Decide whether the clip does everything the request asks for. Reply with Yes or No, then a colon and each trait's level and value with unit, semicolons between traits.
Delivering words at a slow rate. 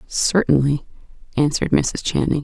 Yes: slow, 100 wpm